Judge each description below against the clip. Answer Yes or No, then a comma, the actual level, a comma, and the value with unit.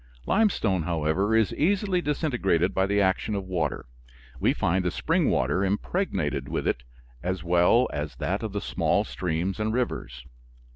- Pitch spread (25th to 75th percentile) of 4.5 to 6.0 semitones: Yes, average, 5.1 semitones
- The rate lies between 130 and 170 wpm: Yes, average, 155 wpm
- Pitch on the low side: Yes, very low, 95 Hz